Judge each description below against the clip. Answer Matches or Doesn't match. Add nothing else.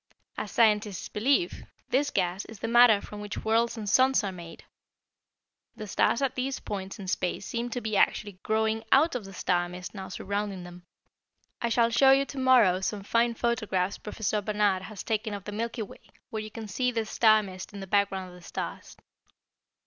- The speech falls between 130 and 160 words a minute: Doesn't match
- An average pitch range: Matches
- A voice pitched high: Matches